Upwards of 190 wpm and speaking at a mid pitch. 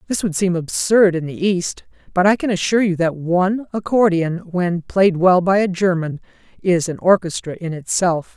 No: average, 185 wpm; medium, 180 Hz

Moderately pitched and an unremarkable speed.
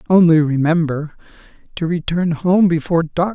No: medium, 165 Hz; slow, 125 wpm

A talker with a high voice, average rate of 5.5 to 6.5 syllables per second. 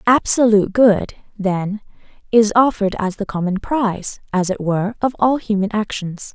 No: high, 210 Hz; 4.9 syllables/s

